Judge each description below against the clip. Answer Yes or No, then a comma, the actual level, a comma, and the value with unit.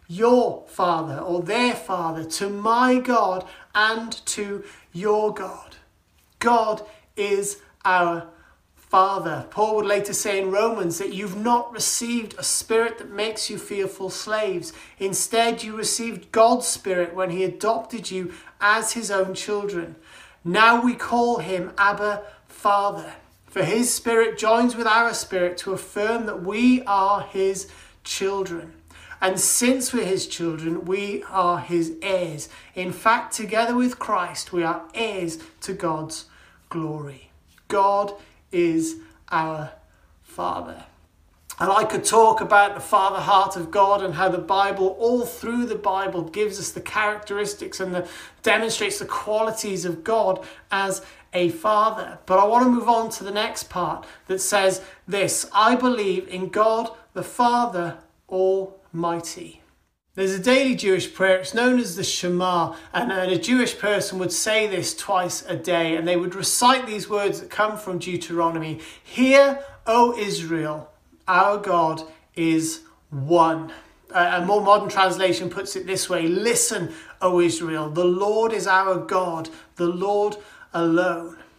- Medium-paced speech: Yes, average, 150 wpm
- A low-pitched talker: No, high, 195 Hz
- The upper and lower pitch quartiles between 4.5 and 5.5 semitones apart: No, average, 3.8 semitones